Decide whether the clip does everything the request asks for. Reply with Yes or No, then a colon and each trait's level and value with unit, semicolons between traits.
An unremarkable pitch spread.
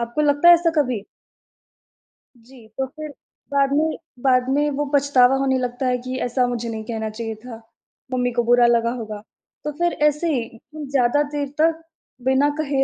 Yes: average, 3.4 semitones